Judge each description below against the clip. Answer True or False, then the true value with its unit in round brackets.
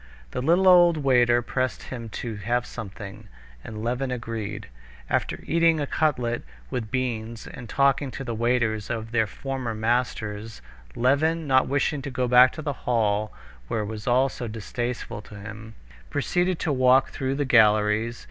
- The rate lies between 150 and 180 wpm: True (165 wpm)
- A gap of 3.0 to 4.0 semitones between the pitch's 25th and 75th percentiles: True (3.5 semitones)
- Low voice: True (120 Hz)